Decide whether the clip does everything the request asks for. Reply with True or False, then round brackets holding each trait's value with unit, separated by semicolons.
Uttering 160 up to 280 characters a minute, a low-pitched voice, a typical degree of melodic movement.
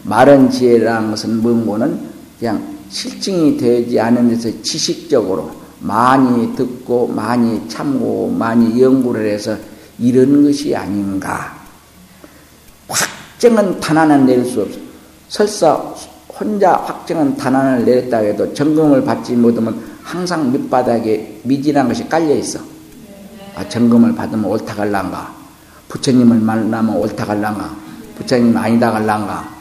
True (265 characters per minute; 120 Hz; 4.2 semitones)